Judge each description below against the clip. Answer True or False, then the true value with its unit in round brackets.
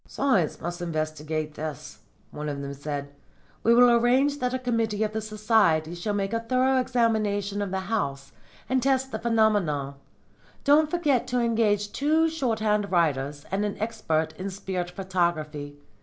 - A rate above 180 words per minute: False (155 wpm)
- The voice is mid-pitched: False (205 Hz)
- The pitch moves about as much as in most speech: False (7.0 semitones)